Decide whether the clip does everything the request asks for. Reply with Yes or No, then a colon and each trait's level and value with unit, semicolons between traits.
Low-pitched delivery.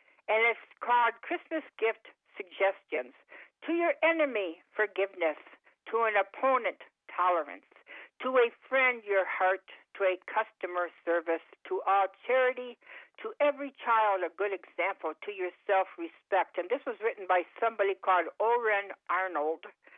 No: high, 215 Hz